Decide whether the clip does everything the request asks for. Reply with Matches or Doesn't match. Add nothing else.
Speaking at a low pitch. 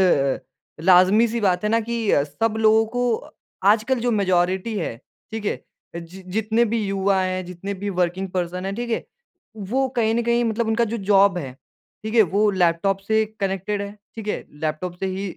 Doesn't match